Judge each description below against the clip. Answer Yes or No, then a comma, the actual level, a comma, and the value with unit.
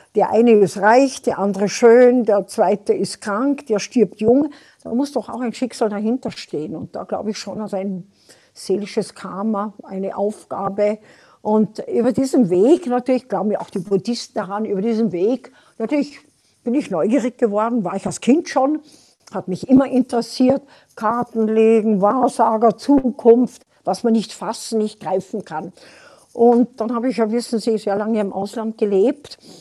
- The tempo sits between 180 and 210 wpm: No, average, 170 wpm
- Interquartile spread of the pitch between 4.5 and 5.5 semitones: No, average, 3.4 semitones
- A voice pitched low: No, high, 225 Hz